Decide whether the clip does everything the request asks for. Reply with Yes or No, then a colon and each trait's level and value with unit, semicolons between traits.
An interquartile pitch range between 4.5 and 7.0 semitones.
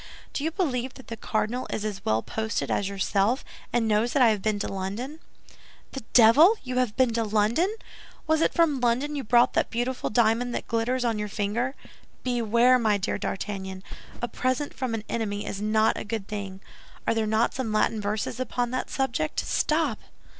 No: average, 3.3 semitones